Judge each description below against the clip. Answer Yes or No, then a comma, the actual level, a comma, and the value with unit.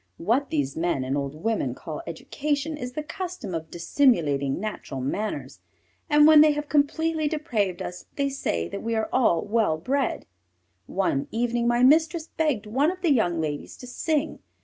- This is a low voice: No, high, 235 Hz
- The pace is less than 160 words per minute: No, average, 170 wpm